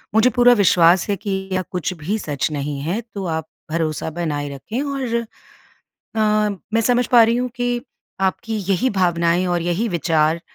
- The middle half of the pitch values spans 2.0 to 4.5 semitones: No, wide, 5.6 semitones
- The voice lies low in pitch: No, medium, 185 Hz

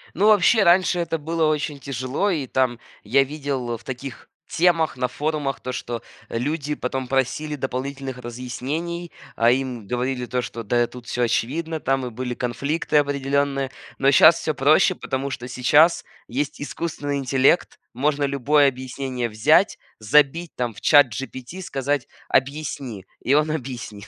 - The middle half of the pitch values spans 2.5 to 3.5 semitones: Yes, average, 3.2 semitones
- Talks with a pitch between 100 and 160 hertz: Yes, low, 135 Hz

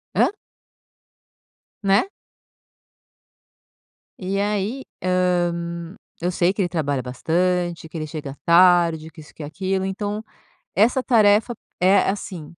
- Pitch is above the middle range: No, medium, 180 Hz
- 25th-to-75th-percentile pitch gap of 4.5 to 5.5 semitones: No, average, 3.1 semitones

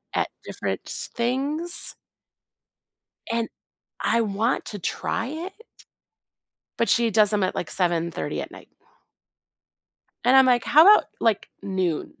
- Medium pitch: No, high, 230 Hz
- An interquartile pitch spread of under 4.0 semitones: No, average, 5.2 semitones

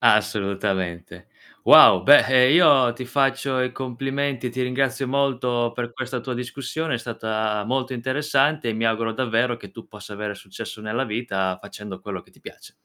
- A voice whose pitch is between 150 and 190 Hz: No, low, 120 Hz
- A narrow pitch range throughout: No, average, 3.5 semitones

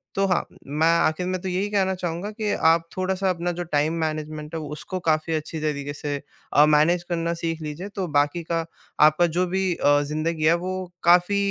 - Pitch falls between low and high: Yes, medium, 165 Hz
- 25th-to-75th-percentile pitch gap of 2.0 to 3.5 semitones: Yes, average, 2.9 semitones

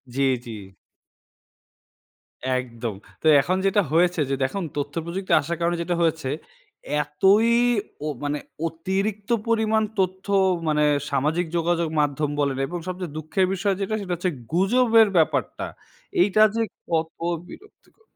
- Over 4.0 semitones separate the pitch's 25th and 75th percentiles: Yes, average, 4.5 semitones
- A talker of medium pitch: Yes, medium, 175 Hz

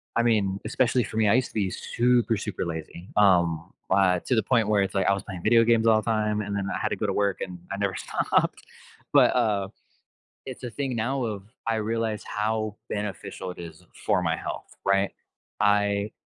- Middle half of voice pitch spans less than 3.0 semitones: Yes, narrow, 2.6 semitones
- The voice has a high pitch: No, low, 105 Hz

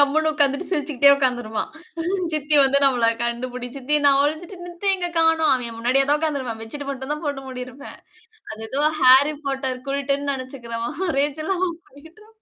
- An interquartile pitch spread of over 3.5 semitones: No, average, 3.1 semitones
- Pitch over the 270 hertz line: Yes, very high, 280 Hz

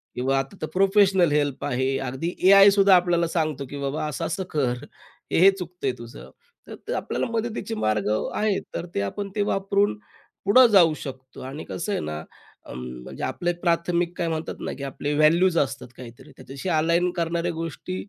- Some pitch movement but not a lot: No, wide, 5.7 semitones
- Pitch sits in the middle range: Yes, medium, 165 Hz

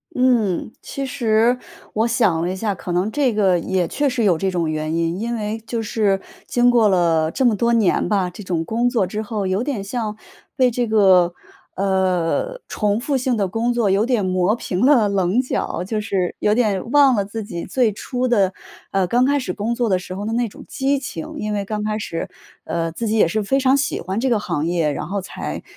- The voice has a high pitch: Yes, high, 210 Hz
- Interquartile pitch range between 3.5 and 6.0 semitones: Yes, average, 4.4 semitones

